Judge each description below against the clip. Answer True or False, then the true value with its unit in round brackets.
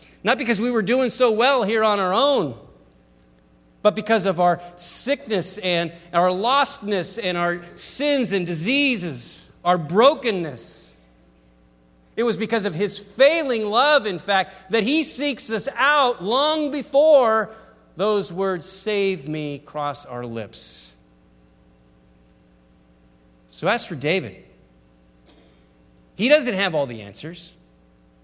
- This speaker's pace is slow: True (125 wpm)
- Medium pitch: True (180 Hz)